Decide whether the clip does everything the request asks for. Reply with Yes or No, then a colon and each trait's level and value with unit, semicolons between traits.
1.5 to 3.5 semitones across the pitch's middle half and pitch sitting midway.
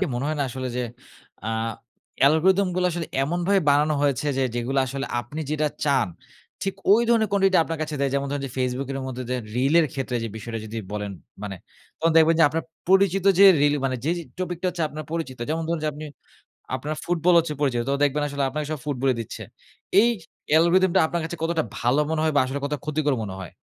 No: average, 3.9 semitones; medium, 150 Hz